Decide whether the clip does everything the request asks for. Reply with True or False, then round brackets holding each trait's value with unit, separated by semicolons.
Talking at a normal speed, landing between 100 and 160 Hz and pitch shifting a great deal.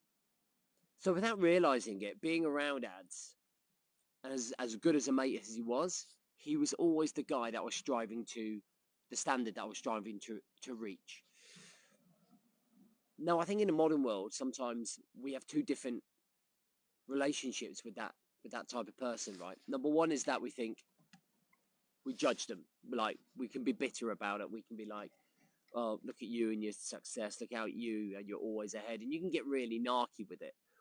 True (190 wpm; 140 Hz; 9.0 semitones)